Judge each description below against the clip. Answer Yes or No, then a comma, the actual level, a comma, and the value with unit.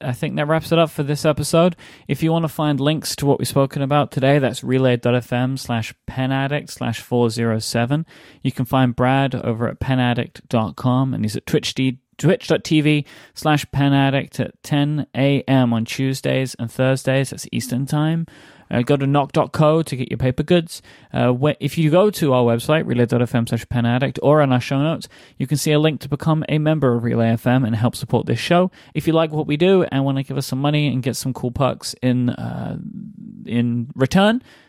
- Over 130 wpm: Yes, average, 200 wpm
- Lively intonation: No, average, 3.5 semitones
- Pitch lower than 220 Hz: Yes, low, 135 Hz